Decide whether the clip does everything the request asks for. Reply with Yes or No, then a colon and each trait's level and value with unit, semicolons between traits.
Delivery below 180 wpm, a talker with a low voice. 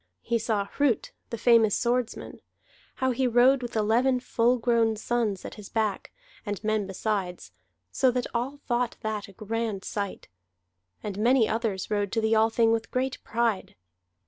No: average, 160 wpm; high, 225 Hz